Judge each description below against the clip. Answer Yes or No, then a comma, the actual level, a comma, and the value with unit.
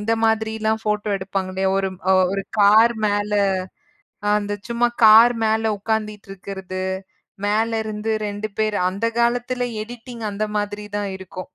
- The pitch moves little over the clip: Yes, narrow, 1.8 semitones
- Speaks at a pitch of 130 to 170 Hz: No, high, 210 Hz